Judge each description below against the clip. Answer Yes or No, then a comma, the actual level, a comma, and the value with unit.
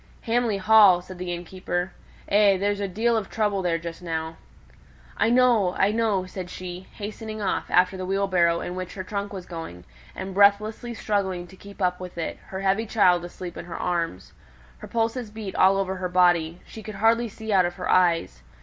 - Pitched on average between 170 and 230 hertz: Yes, high, 190 Hz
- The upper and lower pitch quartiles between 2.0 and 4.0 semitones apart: Yes, average, 2.9 semitones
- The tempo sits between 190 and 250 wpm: Yes, average, 195 wpm